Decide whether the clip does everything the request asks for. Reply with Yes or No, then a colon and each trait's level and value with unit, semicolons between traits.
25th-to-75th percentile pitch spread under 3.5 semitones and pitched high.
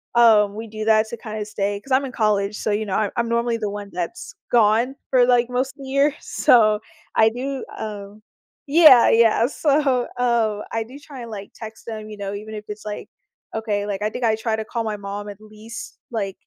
Yes: narrow, 2.5 semitones; high, 220 Hz